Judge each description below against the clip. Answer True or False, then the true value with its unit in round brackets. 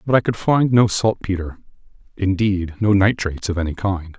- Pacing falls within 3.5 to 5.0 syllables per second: False (5.2 syllables/s)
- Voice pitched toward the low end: True (100 Hz)